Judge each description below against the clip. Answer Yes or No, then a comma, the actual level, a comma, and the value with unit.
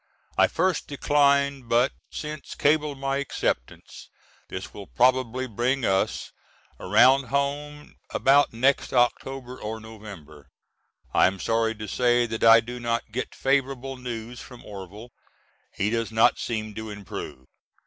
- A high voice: No, low, 120 Hz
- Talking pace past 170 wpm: No, slow, 135 wpm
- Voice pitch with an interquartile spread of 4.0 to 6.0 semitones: No, average, 3.6 semitones